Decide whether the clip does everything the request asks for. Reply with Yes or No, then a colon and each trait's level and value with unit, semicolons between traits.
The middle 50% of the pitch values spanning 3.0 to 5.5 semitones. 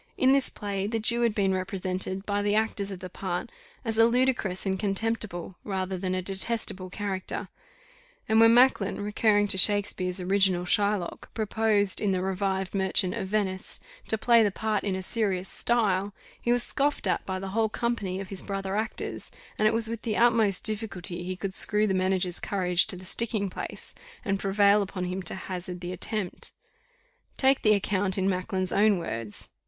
No: narrow, 2.5 semitones